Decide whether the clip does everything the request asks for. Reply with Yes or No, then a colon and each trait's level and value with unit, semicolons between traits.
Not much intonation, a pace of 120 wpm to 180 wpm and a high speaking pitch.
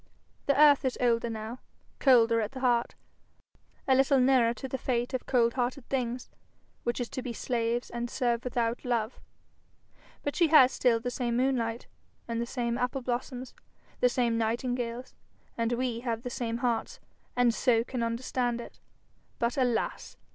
Yes: narrow, 1.6 semitones; average, 160 wpm; high, 245 Hz